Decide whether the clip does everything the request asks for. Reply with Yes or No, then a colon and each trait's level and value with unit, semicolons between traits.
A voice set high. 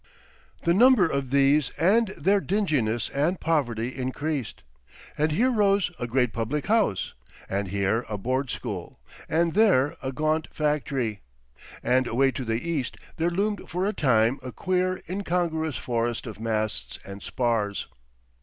No: medium, 140 Hz